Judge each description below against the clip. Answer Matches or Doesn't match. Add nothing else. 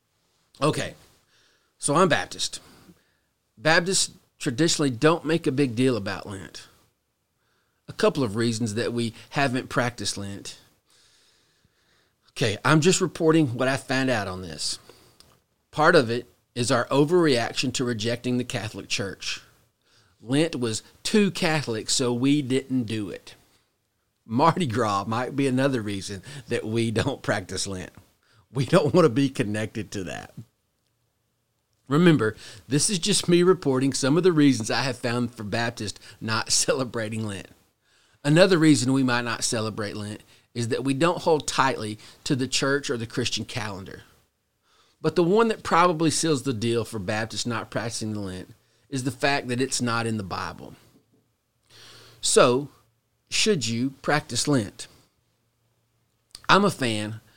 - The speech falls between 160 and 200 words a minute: Doesn't match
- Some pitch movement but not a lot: Matches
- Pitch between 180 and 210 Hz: Doesn't match